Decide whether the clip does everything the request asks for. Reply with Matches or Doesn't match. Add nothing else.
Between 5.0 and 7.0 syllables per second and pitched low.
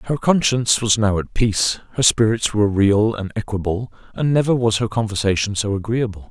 Matches